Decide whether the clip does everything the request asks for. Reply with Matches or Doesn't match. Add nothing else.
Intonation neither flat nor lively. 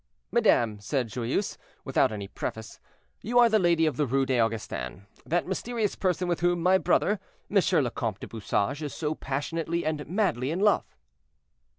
Doesn't match